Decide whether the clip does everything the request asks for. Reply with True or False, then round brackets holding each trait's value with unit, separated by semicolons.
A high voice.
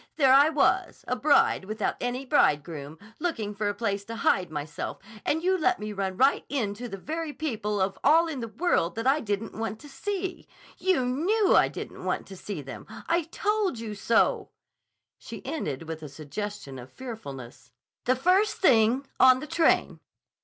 True (230 Hz)